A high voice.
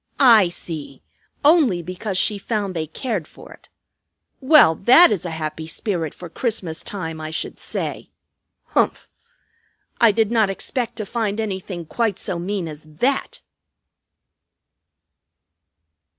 Yes: high, 195 Hz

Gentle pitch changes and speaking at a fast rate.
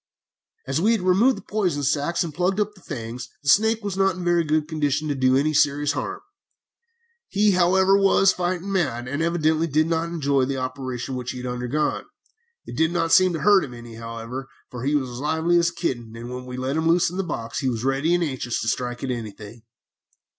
No: wide, 5.6 semitones; fast, 225 wpm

